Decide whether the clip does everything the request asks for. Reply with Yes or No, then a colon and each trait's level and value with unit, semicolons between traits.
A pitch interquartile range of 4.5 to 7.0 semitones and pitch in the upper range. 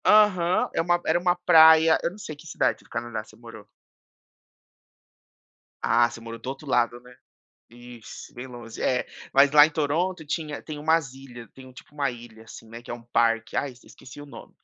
No: average, 5.0 semitones; low, 135 Hz